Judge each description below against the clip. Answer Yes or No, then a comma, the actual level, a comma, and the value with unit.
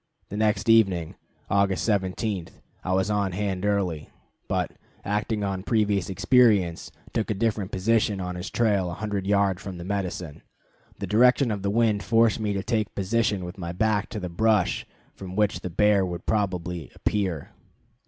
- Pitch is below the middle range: Yes, low, 100 Hz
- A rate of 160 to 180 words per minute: Yes, average, 170 wpm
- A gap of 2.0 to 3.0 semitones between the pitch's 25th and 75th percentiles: Yes, narrow, 2.6 semitones